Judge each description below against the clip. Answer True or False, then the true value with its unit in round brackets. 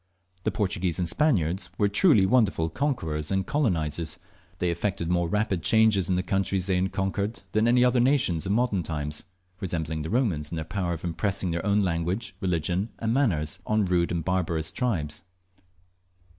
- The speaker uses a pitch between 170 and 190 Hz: False (95 Hz)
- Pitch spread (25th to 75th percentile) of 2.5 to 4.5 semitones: True (4.1 semitones)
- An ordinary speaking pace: True (170 wpm)